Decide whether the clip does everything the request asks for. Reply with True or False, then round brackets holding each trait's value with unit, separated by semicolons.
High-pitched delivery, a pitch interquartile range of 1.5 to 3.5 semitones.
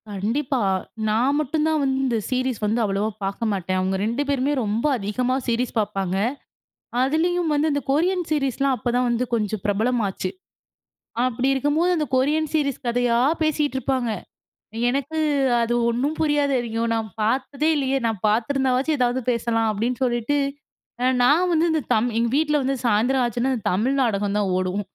False (250 Hz; 4.3 semitones)